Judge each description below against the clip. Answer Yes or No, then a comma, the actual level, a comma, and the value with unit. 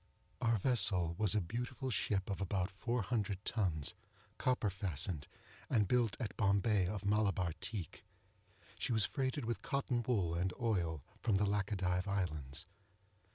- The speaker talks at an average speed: Yes, average, 145 wpm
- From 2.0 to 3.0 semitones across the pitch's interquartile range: No, average, 3.9 semitones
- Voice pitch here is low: Yes, low, 100 Hz